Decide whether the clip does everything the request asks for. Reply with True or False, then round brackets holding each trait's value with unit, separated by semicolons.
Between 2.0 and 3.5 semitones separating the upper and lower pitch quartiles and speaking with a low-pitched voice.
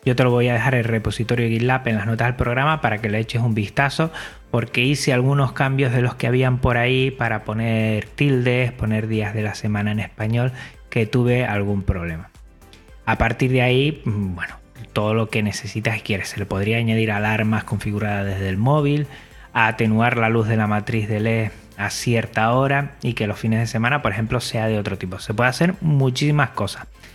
True (2.8 semitones; 115 Hz)